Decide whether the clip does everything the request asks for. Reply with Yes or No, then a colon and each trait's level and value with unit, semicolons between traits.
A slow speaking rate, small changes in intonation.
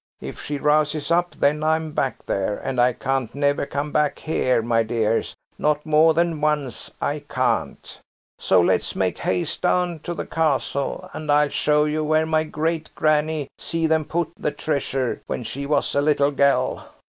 No: average, 175 wpm; narrow, 2.1 semitones